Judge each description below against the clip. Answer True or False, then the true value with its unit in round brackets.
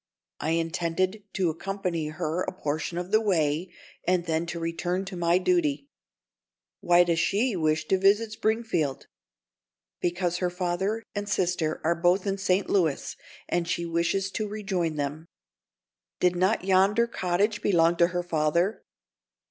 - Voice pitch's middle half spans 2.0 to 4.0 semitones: True (2.8 semitones)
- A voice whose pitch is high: False (175 Hz)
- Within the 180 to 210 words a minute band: False (150 wpm)